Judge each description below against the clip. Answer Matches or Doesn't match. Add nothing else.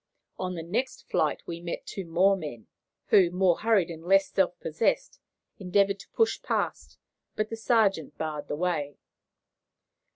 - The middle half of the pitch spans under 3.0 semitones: Doesn't match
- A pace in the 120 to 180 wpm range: Matches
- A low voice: Doesn't match